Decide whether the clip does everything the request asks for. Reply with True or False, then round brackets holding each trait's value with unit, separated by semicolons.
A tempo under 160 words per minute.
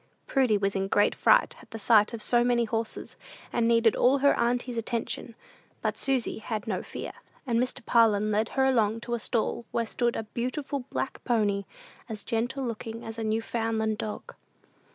False (180 wpm)